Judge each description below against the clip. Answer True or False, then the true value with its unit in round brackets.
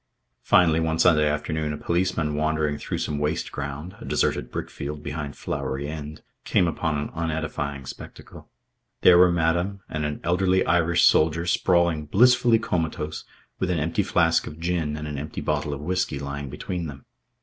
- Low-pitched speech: True (80 Hz)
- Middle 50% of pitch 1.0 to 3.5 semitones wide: True (2.7 semitones)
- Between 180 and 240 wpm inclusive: False (165 wpm)